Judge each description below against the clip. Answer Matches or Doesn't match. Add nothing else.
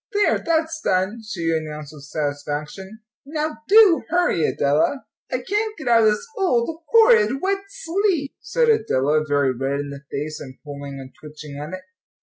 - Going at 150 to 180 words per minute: Matches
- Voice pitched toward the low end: Doesn't match